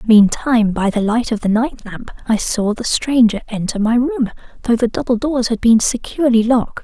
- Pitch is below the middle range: No, high, 230 Hz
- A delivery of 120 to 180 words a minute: No, average, 200 wpm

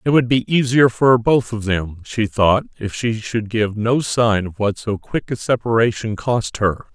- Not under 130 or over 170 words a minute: No, fast, 205 wpm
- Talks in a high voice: No, low, 115 Hz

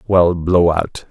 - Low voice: Yes, very low, 85 Hz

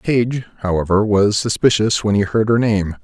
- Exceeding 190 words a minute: Yes, average, 200 wpm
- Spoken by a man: Yes, male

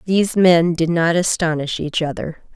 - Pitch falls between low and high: Yes, medium, 170 Hz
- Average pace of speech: Yes, average, 165 wpm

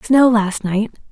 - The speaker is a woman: Yes, female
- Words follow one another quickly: No, average, 160 wpm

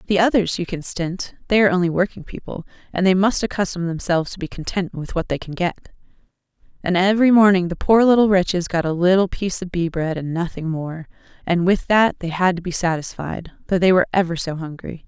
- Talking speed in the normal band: No, fast, 215 wpm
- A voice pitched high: No, medium, 180 Hz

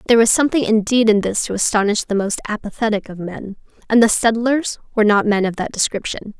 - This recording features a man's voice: No, female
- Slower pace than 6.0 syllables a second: No, 6.2 syllables/s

